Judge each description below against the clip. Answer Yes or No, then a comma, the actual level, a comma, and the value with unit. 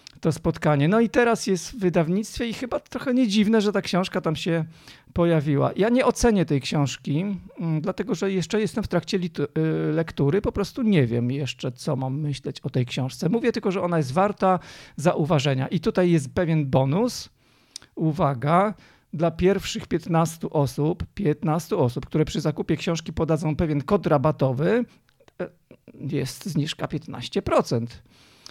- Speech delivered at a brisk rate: No, average, 150 wpm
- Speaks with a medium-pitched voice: Yes, medium, 170 Hz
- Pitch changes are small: No, average, 5.2 semitones